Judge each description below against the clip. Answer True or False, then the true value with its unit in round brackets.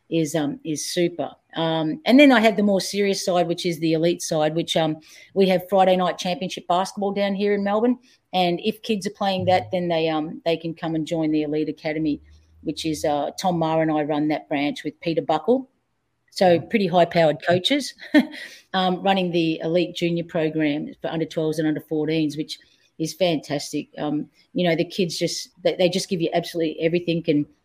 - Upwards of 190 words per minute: True (200 wpm)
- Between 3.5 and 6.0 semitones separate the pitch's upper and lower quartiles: False (3.1 semitones)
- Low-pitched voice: False (170 Hz)